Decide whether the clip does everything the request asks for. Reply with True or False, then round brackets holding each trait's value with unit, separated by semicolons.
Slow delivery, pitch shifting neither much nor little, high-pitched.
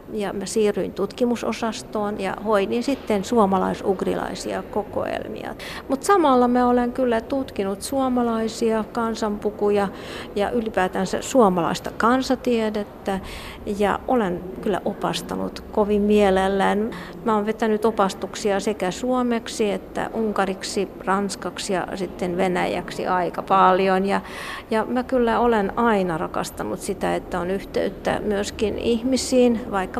False (110 wpm; 3.5 semitones; 210 Hz)